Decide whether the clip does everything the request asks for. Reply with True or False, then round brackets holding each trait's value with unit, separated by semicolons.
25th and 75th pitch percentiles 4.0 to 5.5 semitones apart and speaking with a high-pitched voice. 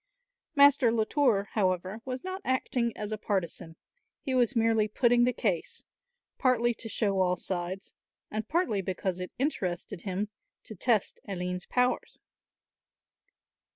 True (4.9 semitones; 215 Hz)